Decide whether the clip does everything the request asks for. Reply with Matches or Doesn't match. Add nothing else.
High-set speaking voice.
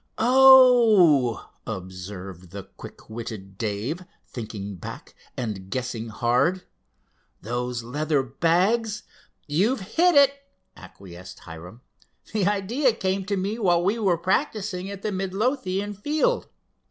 Doesn't match